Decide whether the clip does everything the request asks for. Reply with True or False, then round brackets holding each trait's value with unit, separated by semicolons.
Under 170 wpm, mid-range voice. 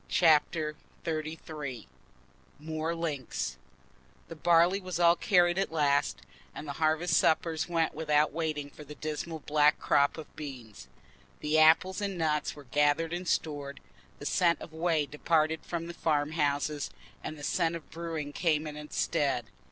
True (160 wpm; 155 Hz)